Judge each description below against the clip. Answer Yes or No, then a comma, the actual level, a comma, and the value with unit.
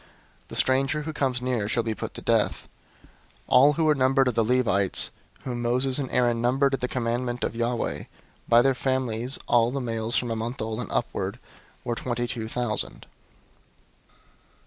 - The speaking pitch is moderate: No, low, 125 Hz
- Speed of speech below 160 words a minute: No, average, 180 wpm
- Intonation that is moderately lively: No, narrow, 2.1 semitones